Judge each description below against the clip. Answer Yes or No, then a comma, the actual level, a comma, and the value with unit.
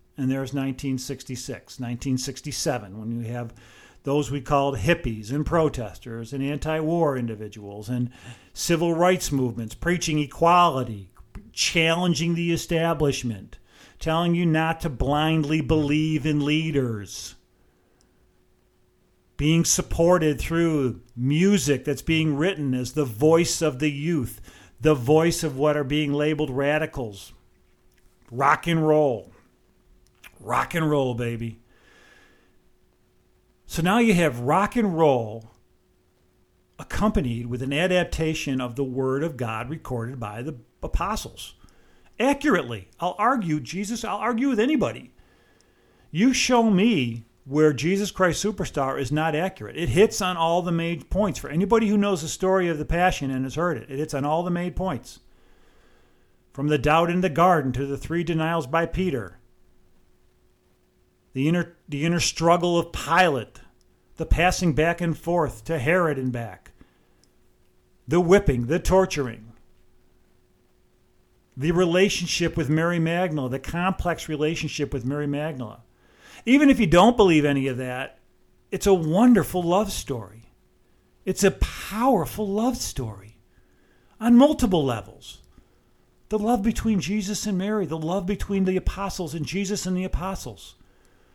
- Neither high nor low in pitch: Yes, medium, 155 Hz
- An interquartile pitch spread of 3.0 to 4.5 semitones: No, wide, 5.4 semitones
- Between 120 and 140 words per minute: Yes, slow, 135 wpm